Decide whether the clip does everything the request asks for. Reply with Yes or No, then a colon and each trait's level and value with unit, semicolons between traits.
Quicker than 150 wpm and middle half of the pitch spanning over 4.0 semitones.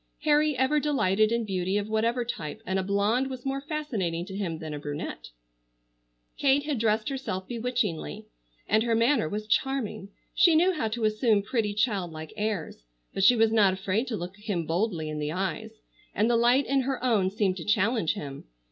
Yes: average, 190 wpm; average, 4.7 semitones